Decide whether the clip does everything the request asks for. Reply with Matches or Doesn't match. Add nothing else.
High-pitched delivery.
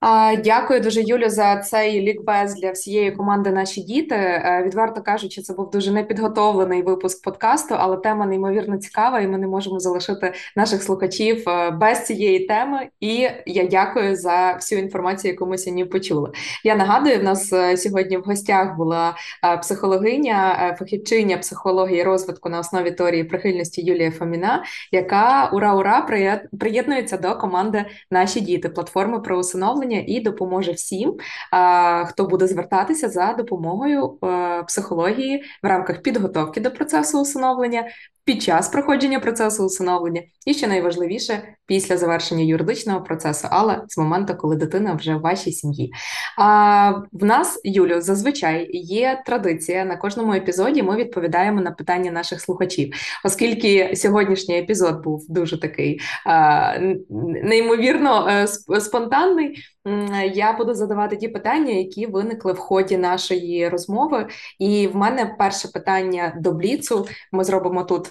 Matches